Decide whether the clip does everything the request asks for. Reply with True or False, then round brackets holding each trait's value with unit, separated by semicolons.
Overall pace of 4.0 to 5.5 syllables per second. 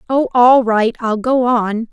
False (3.7 syllables/s)